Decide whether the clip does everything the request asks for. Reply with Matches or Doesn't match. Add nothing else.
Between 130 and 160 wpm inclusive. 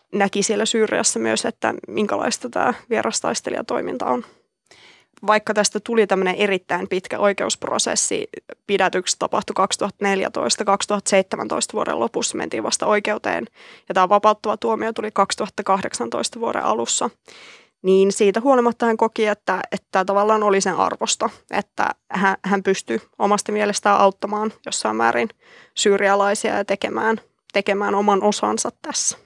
Doesn't match